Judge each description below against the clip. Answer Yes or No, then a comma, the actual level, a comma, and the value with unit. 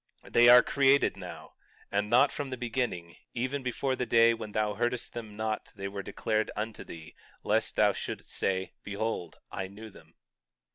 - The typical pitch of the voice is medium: No, low, 110 Hz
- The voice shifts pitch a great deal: No, average, 3.5 semitones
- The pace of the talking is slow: No, average, 175 wpm